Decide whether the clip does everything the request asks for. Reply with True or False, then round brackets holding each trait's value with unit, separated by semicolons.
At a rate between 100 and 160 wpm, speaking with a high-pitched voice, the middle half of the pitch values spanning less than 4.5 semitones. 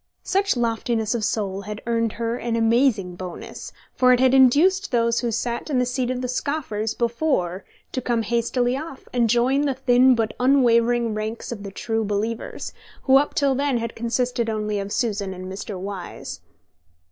False (180 wpm; 235 Hz; 2.9 semitones)